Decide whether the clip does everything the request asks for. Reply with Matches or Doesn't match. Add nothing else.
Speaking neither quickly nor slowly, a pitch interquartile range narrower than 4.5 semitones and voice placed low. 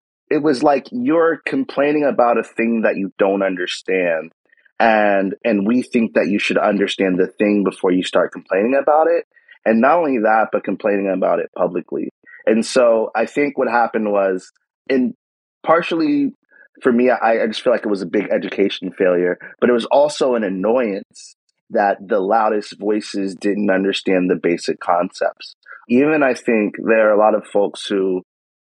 Doesn't match